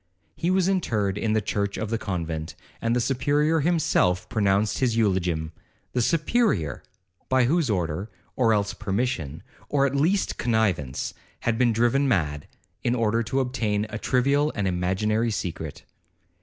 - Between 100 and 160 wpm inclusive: Yes, average, 150 wpm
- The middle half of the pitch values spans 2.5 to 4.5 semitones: No, wide, 5.6 semitones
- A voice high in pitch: No, low, 110 Hz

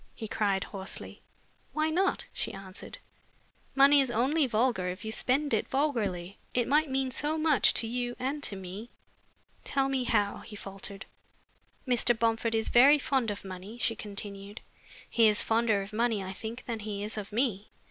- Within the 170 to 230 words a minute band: Yes, average, 175 wpm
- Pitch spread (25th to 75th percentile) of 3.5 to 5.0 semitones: Yes, average, 4.6 semitones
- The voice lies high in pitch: Yes, high, 225 Hz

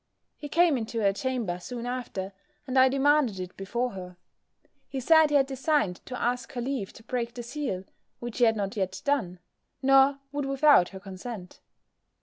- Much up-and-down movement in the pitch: Yes, wide, 5.7 semitones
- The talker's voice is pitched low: No, high, 245 Hz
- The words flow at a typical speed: Yes, average, 180 wpm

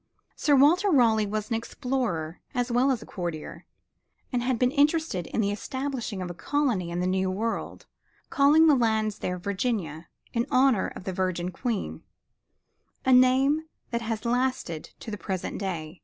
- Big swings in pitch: Yes, wide, 5.8 semitones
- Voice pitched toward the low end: No, high, 225 Hz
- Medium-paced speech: Yes, average, 170 wpm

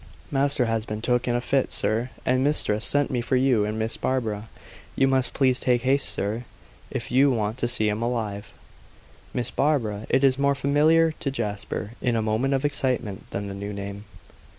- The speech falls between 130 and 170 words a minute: No, average, 195 wpm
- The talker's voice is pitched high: No, low, 120 Hz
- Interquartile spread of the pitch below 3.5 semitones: No, average, 3.9 semitones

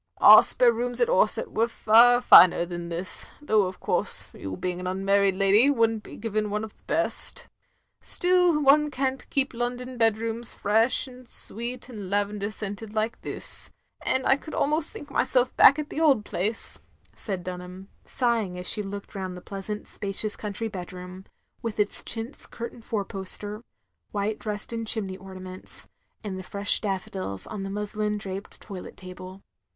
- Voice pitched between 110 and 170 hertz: No, high, 210 Hz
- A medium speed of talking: Yes, average, 170 wpm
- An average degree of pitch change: Yes, average, 3.7 semitones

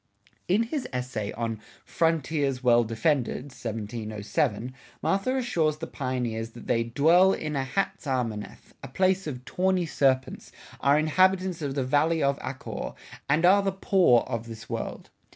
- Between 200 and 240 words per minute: No, average, 145 wpm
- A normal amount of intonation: No, wide, 6.4 semitones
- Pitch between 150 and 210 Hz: No, medium, 140 Hz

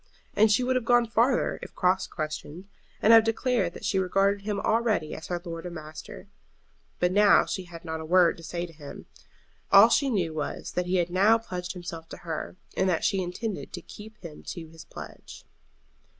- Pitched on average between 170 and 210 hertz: Yes, medium, 185 Hz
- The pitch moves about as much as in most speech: Yes, average, 4.2 semitones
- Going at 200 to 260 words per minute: Yes, fast, 205 wpm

